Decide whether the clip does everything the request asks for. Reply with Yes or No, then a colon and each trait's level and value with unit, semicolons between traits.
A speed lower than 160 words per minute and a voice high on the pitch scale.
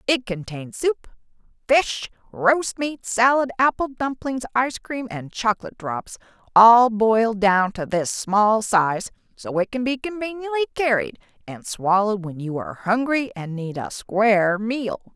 Yes: average, 150 wpm; high, 225 Hz